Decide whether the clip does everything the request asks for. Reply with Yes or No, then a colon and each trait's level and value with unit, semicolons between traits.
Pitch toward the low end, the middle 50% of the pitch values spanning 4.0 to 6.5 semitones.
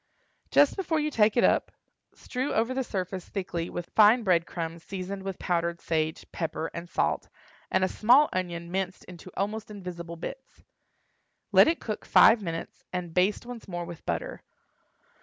No: medium, 185 Hz; average, 4.3 semitones